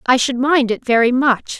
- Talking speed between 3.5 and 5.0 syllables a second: Yes, 4.8 syllables/s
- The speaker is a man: No, female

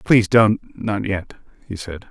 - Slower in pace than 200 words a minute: Yes, average, 140 wpm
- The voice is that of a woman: No, male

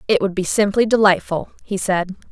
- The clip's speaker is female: Yes, female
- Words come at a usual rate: Yes, average, 180 wpm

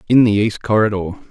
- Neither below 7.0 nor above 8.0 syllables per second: No, 6.3 syllables/s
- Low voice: Yes, low, 115 Hz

